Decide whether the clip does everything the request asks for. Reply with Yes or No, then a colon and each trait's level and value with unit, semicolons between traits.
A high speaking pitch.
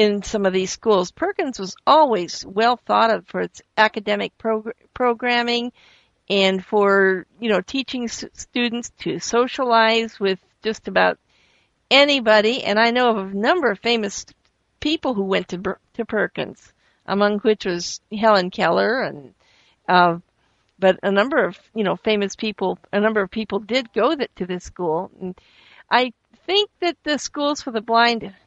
Yes: high, 215 Hz